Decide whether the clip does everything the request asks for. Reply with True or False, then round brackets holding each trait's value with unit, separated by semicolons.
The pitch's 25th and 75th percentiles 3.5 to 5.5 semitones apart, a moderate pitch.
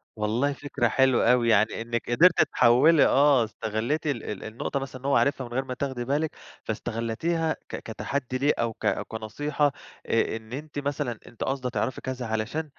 False (3.8 semitones; 130 Hz)